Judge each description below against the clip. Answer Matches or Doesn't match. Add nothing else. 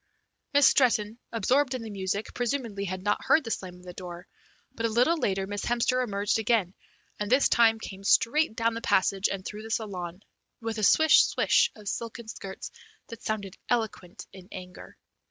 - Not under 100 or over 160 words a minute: Doesn't match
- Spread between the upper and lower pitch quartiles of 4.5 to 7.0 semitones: Doesn't match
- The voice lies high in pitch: Matches